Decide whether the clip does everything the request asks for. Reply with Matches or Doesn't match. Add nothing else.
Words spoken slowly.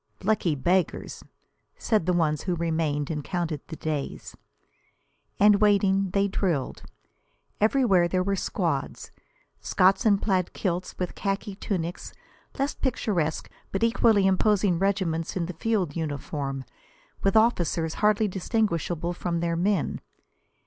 Matches